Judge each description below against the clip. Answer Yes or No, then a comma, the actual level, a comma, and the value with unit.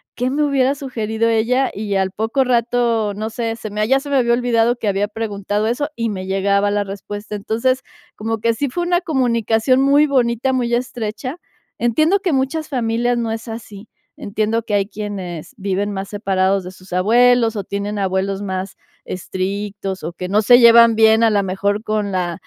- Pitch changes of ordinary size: Yes, average, 3.3 semitones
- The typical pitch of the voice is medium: No, high, 220 Hz